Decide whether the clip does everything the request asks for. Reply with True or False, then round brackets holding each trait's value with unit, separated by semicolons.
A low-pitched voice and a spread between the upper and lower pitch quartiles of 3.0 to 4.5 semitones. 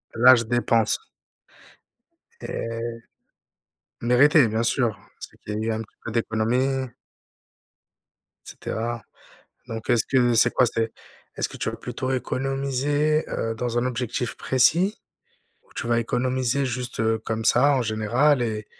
False (120 Hz; 2.5 semitones)